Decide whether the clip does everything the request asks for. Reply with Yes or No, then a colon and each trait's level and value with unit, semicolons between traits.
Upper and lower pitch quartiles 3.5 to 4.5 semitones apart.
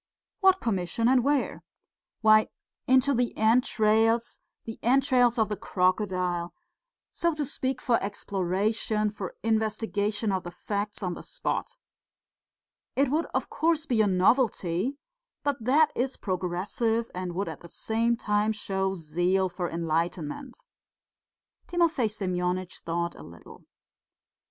No: average, 5.2 semitones